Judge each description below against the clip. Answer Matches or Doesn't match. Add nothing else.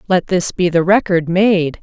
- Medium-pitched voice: Matches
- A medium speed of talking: Matches